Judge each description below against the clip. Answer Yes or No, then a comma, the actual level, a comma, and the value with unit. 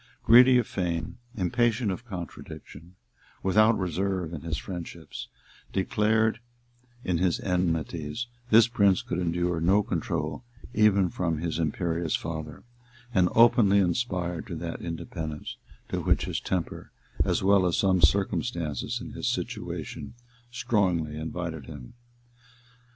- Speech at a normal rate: No, slow, 125 wpm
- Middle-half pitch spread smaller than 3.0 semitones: No, average, 3.8 semitones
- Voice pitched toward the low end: Yes, very low, 90 Hz